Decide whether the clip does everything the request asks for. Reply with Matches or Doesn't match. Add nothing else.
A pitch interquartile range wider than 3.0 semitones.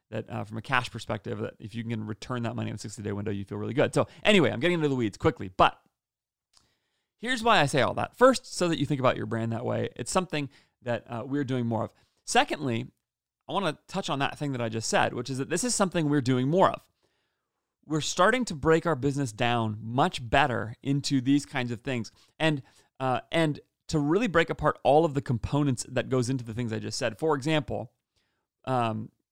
Matches